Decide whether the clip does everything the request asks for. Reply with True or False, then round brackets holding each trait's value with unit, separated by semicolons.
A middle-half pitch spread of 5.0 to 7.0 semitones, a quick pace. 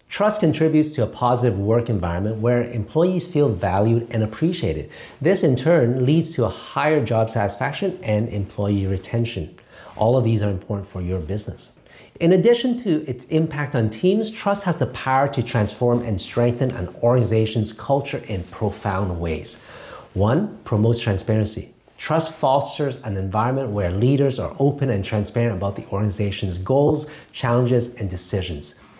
False (5.5 semitones; 155 wpm)